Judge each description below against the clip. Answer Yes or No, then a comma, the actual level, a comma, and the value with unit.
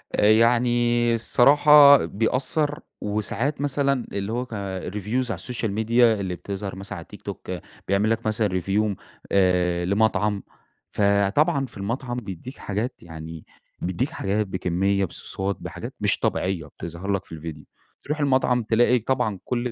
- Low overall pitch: Yes, low, 110 Hz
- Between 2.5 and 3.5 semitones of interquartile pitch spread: No, average, 4.1 semitones